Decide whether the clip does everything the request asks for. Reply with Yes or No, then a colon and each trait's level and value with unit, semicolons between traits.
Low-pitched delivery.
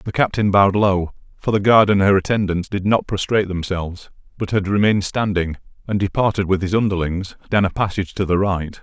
Yes: very low, 95 Hz